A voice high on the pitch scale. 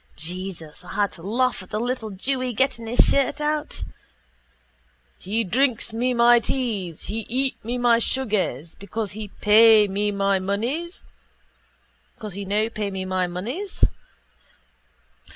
Yes: high, 225 Hz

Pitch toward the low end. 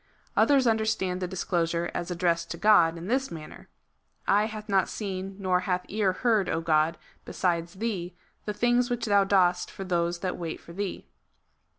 No: medium, 185 Hz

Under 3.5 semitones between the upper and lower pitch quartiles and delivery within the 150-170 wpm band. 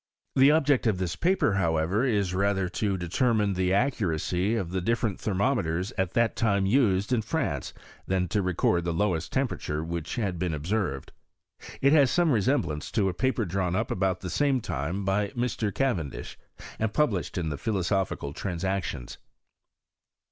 No: average, 4.7 semitones; average, 165 wpm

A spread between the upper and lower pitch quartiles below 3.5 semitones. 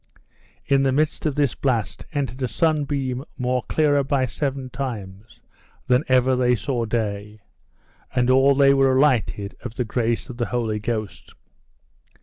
Yes: average, 2.9 semitones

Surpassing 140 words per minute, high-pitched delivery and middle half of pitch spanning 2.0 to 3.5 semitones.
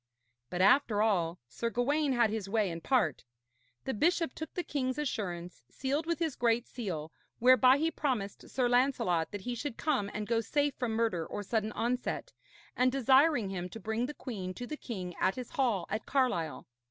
No: average, 190 wpm; high, 235 Hz; average, 5.1 semitones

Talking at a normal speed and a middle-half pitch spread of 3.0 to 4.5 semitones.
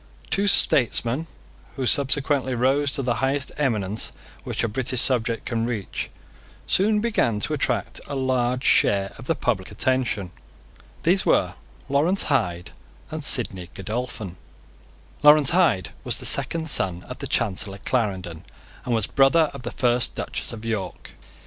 No: average, 145 wpm; average, 4.9 semitones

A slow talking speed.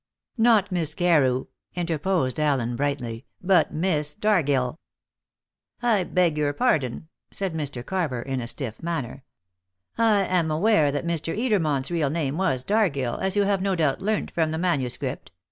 No: average, 150 wpm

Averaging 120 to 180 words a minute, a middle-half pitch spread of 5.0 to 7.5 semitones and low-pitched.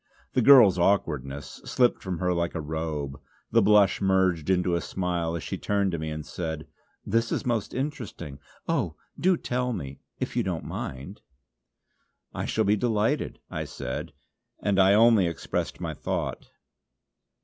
Yes: average, 160 wpm; average, 5.3 semitones; very low, 95 Hz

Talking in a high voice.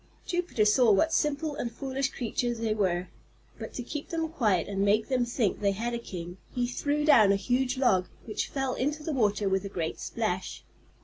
Yes: high, 235 Hz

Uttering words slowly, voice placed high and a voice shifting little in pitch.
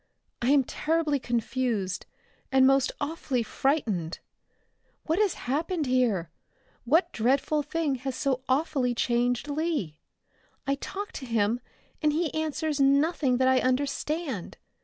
No: slow, 125 wpm; very high, 270 Hz; average, 3.8 semitones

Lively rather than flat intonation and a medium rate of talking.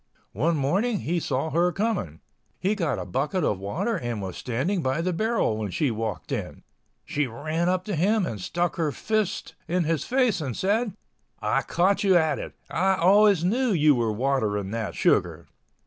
Yes: wide, 7.3 semitones; average, 180 wpm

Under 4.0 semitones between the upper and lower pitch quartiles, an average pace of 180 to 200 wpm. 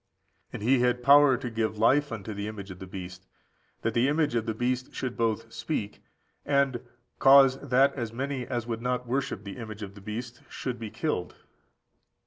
Yes: average, 3.5 semitones; average, 190 wpm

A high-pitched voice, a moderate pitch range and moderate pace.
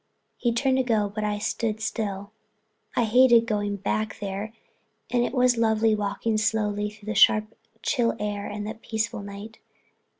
No: high, 215 Hz; narrow, 1.9 semitones; average, 170 wpm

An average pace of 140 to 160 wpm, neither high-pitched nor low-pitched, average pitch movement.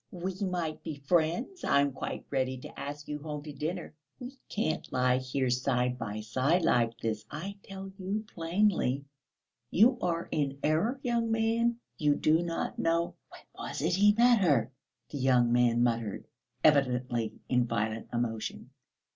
No: average, 155 wpm; medium, 150 Hz; wide, 6.8 semitones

